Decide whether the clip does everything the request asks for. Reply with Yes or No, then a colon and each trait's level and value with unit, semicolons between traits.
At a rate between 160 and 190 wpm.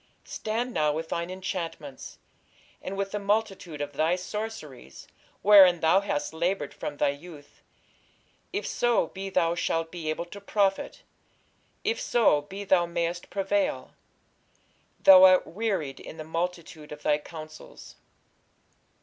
No: slow, 135 wpm